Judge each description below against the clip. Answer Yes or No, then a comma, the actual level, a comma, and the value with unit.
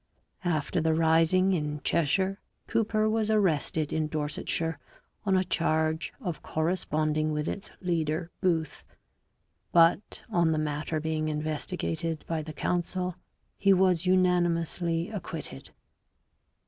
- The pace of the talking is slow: Yes, slow, 115 wpm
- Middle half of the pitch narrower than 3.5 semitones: Yes, average, 2.9 semitones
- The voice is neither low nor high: Yes, medium, 165 Hz